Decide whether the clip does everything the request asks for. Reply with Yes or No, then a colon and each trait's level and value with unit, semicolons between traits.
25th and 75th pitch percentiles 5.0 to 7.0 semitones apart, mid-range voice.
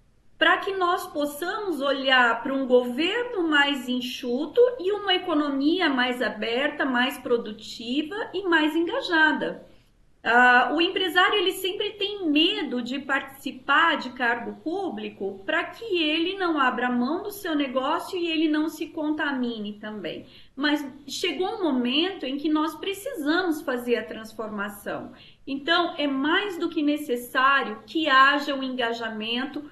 No: wide, 5.4 semitones; very high, 295 Hz